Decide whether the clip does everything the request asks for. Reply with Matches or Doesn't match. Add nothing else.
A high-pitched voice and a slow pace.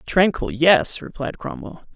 Doesn't match